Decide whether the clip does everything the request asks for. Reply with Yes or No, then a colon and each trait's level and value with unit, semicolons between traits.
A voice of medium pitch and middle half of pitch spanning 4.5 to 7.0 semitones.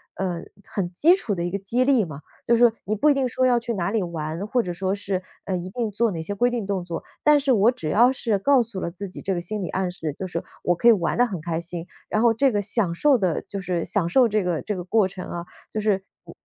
No: high, 200 Hz; average, 5.0 semitones